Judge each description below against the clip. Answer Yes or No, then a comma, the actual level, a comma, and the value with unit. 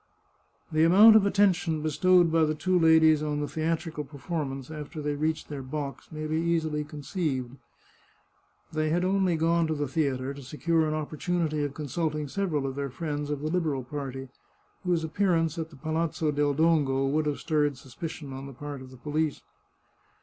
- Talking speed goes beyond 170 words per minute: Yes, average, 180 wpm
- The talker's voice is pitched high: No, medium, 155 Hz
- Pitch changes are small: Yes, narrow, 2.3 semitones